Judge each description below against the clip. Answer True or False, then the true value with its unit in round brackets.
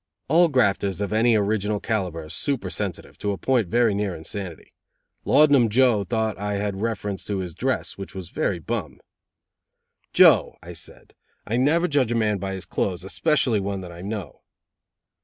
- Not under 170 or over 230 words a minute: True (175 wpm)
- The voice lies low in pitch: True (105 Hz)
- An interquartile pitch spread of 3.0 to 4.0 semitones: True (3.6 semitones)